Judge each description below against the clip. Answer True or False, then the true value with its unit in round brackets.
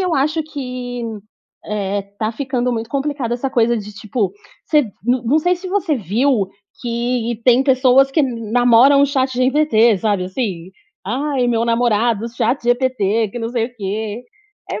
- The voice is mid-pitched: False (245 Hz)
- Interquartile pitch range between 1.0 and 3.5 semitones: True (3.2 semitones)